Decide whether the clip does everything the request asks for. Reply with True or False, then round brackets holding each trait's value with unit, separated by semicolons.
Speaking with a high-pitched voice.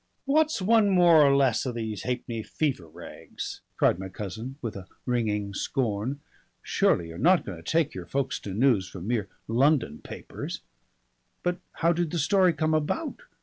False (130 Hz)